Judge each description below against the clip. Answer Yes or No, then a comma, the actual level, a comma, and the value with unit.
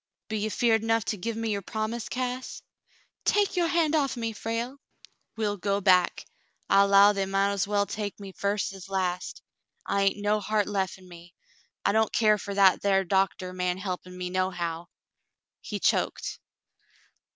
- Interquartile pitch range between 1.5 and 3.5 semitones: Yes, average, 2.7 semitones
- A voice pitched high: Yes, high, 200 Hz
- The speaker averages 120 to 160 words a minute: No, average, 175 wpm